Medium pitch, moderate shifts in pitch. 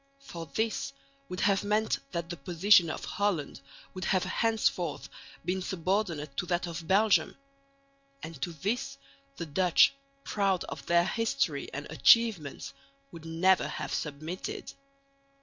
Yes: medium, 180 Hz; average, 3.8 semitones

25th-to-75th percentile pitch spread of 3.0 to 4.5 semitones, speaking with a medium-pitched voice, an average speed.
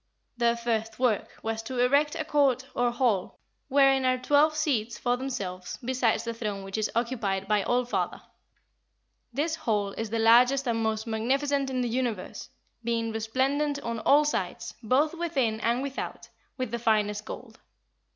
No: average, 3.4 semitones; high, 240 Hz; average, 160 wpm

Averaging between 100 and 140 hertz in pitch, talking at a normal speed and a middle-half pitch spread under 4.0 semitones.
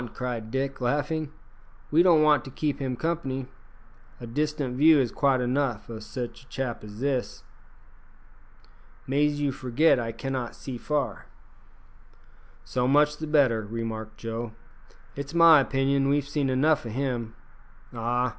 Yes: low, 135 Hz; average, 145 wpm; average, 3.6 semitones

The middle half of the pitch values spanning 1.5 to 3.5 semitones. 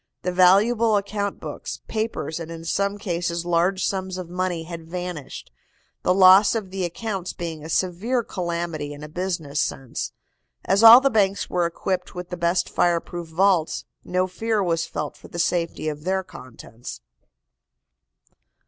Yes: narrow, 2.6 semitones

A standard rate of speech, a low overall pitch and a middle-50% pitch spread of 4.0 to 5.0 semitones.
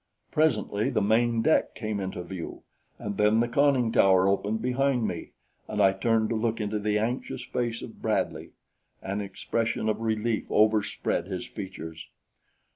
No: average, 155 wpm; low, 110 Hz; average, 2.9 semitones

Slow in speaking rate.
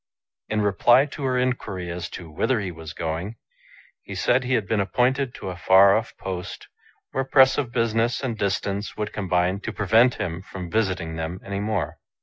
No: average, 185 wpm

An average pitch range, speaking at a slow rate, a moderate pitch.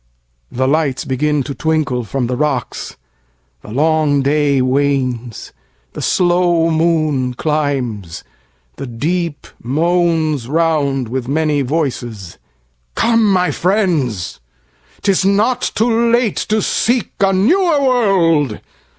No: wide, 5.8 semitones; slow, 105 wpm; medium, 150 Hz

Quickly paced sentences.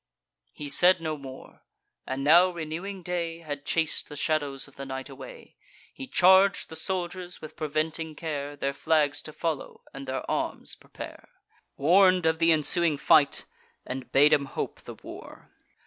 No: average, 160 wpm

